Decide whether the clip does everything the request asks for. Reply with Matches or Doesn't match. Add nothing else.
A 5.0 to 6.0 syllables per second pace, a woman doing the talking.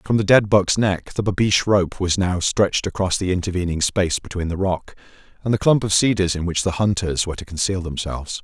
Doesn't match